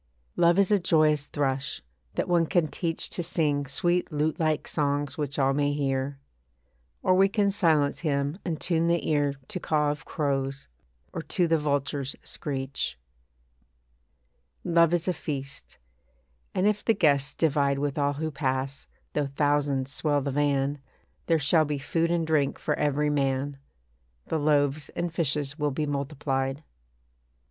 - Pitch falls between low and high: Yes, medium, 145 Hz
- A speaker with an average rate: Yes, average, 155 wpm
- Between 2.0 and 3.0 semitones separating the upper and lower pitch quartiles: Yes, average, 2.7 semitones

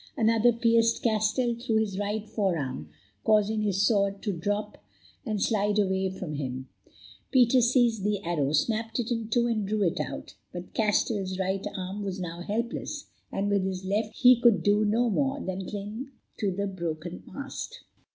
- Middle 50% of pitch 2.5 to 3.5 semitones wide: Yes, average, 3.2 semitones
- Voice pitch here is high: Yes, high, 205 Hz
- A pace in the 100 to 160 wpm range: No, average, 170 wpm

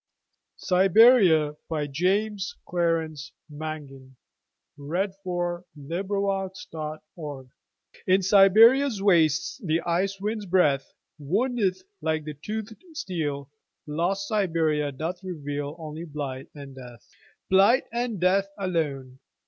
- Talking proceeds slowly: Yes, slow, 80 wpm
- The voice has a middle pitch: Yes, medium, 170 Hz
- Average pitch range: Yes, average, 4.7 semitones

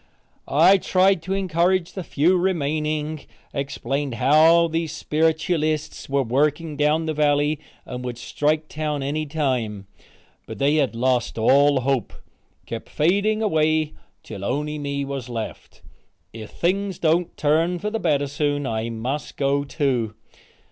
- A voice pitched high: No, medium, 150 Hz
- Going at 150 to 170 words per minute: No, average, 140 wpm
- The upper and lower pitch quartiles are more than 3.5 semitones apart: No, average, 2.9 semitones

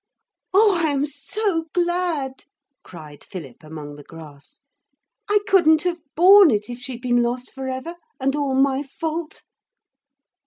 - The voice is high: Yes, very high, 275 Hz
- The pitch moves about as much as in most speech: No, wide, 5.9 semitones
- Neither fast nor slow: Yes, average, 145 wpm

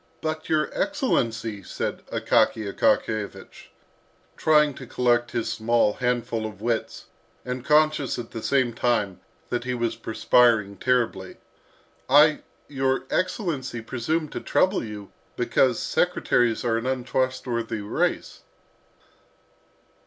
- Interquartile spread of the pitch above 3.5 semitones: No, average, 3.1 semitones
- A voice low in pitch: Yes, low, 120 Hz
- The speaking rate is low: Yes, slow, 115 wpm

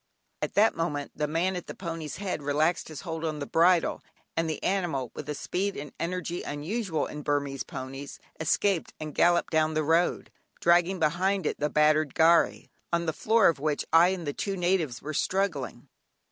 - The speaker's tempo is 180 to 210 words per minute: Yes, average, 190 wpm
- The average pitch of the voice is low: No, medium, 160 Hz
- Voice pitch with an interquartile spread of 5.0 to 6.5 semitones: No, average, 3.1 semitones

